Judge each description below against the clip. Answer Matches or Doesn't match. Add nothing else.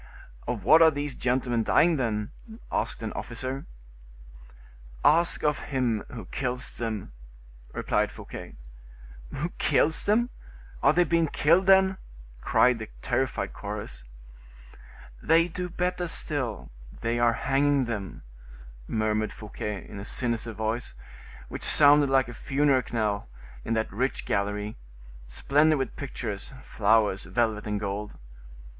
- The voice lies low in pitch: Matches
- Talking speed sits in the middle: Doesn't match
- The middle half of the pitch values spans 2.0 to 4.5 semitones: Doesn't match